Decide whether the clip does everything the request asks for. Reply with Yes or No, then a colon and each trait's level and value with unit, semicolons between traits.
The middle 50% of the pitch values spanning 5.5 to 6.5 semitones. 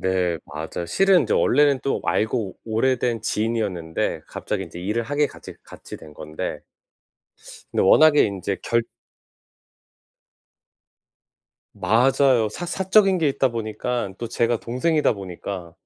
Yes: wide, 6.1 semitones